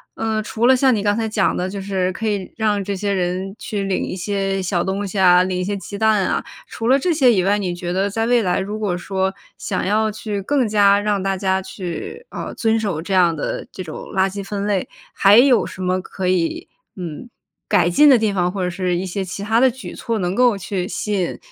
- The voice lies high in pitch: Yes, high, 200 Hz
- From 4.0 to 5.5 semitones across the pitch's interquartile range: No, average, 2.7 semitones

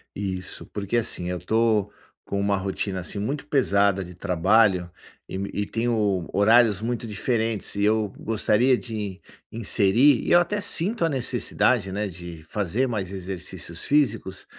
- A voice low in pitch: Yes, low, 105 Hz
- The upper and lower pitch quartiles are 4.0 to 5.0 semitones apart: No, average, 3.6 semitones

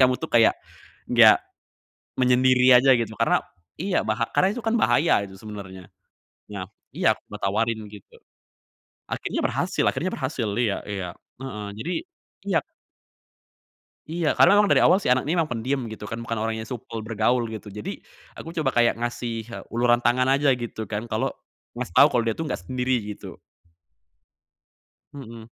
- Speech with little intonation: No, average, 3.4 semitones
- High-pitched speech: No, low, 120 Hz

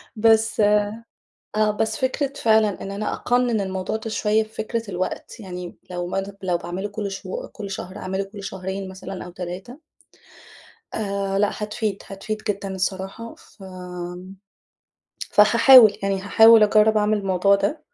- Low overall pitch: No, high, 200 Hz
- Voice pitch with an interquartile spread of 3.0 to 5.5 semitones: No, narrow, 2.5 semitones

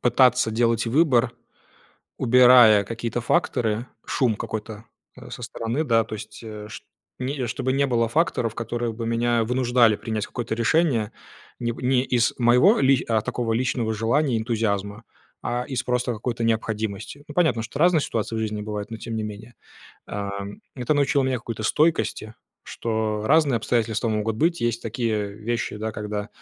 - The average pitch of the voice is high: No, low, 115 Hz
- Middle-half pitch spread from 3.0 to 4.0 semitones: No, narrow, 2.5 semitones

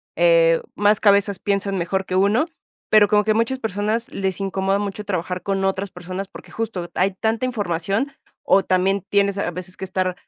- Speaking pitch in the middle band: No, high, 200 Hz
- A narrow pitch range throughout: Yes, narrow, 2.2 semitones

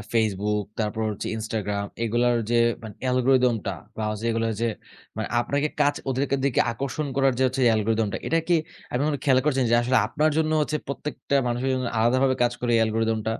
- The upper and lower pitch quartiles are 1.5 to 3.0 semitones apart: No, average, 3.4 semitones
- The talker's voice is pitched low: Yes, low, 120 Hz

